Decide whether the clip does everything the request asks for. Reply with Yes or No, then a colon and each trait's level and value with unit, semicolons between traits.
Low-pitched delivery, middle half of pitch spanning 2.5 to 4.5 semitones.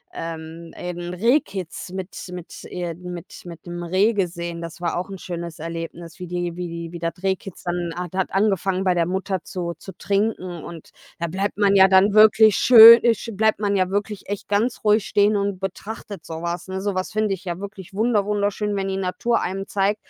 No: high, 190 Hz; average, 2.8 semitones